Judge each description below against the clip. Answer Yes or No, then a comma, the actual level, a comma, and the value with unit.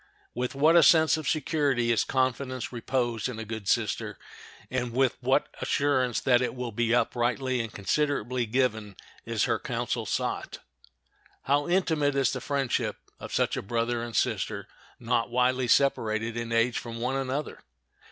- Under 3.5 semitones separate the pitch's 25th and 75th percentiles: Yes, average, 2.8 semitones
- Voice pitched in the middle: No, low, 125 Hz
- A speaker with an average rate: Yes, average, 160 wpm